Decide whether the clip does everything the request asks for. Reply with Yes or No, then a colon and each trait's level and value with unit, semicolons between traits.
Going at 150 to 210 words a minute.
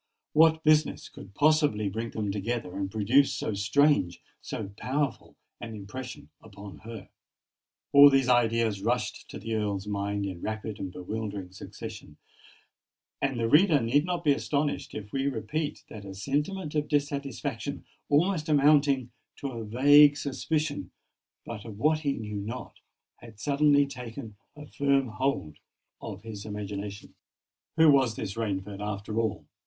No: average, 140 wpm